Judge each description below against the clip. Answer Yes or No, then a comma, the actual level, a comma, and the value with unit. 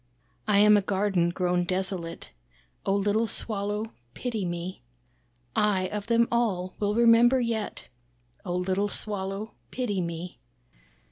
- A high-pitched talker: Yes, high, 200 Hz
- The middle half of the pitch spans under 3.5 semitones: Yes, average, 2.8 semitones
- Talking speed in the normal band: No, slow, 125 wpm